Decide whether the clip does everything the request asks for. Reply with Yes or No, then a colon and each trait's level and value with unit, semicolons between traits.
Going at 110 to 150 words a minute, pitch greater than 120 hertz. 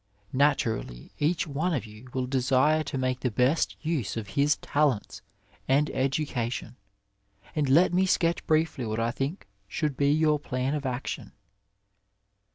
Yes: average, 145 wpm; low, 135 Hz